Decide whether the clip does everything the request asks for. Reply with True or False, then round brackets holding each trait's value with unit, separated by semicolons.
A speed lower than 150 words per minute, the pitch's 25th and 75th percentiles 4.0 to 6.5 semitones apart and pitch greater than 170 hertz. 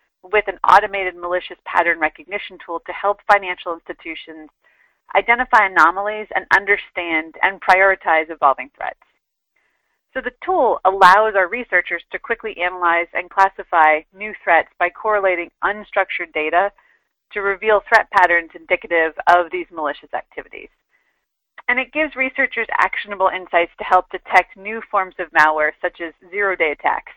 False (140 wpm; 3.5 semitones; 185 Hz)